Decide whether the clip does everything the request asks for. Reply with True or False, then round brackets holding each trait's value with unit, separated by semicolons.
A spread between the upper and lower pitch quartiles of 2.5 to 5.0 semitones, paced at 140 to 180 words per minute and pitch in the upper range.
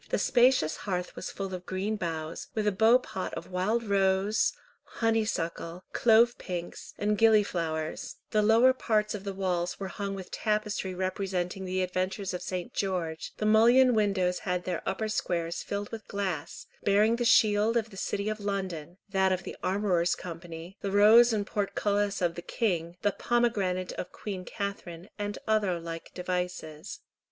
True (2.9 semitones; 165 wpm; 195 Hz)